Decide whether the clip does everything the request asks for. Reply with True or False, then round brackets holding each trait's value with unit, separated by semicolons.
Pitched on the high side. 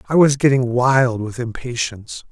False (125 Hz)